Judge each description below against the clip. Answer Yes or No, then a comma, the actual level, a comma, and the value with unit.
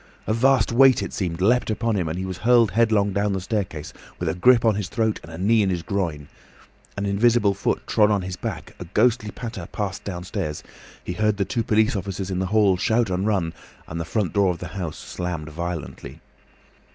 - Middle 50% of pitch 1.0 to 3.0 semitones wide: No, average, 3.5 semitones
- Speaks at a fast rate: Yes, fast, 215 wpm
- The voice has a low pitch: Yes, low, 100 Hz